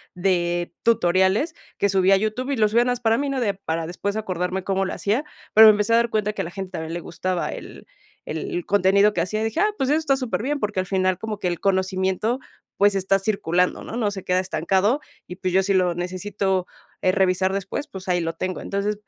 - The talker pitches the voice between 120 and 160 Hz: No, high, 195 Hz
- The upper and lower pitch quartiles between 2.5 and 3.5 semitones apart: Yes, average, 2.8 semitones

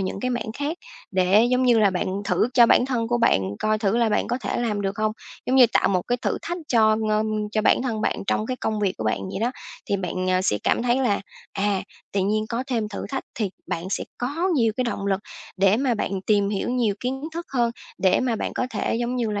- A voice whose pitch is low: No, high, 220 Hz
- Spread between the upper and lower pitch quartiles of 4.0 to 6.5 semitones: No, average, 3.5 semitones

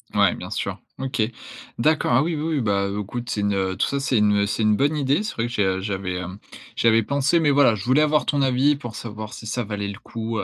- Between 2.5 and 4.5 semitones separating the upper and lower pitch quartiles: No, wide, 5.4 semitones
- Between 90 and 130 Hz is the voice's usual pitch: Yes, low, 115 Hz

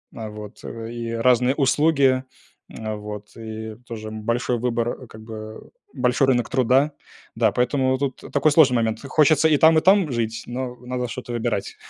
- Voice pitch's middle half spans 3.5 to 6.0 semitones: No, average, 3.0 semitones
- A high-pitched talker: No, low, 125 Hz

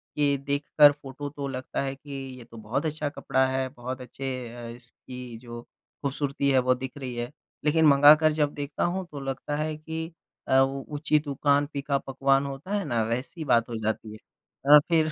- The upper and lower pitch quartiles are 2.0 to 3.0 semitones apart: Yes, narrow, 2.5 semitones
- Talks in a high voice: No, medium, 140 Hz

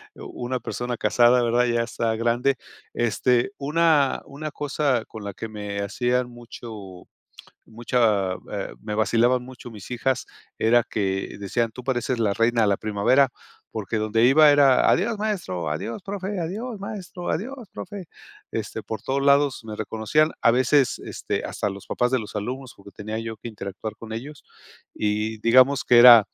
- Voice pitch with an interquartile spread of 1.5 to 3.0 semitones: No, average, 4.1 semitones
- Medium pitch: No, low, 120 Hz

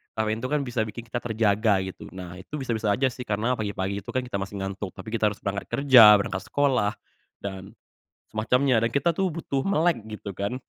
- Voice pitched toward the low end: Yes, low, 110 Hz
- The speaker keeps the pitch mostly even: No, average, 4.1 semitones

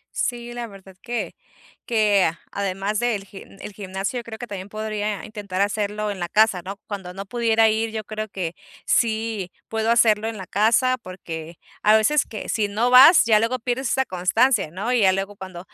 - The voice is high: Yes, high, 215 Hz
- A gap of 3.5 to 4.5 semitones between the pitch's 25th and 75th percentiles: No, average, 2.8 semitones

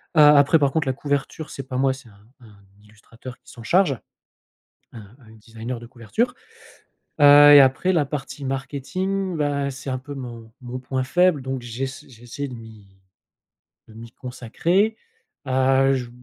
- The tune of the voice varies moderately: Yes, average, 3.5 semitones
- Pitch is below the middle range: Yes, low, 130 Hz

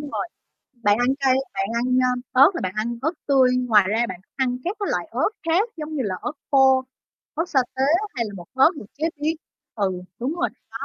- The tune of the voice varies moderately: Yes, average, 4.9 semitones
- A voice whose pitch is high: Yes, very high, 260 Hz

